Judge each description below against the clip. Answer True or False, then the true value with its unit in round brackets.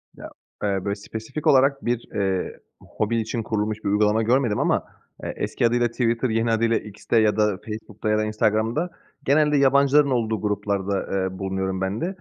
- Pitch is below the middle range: True (110 Hz)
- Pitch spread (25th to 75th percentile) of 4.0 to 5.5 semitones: False (2.8 semitones)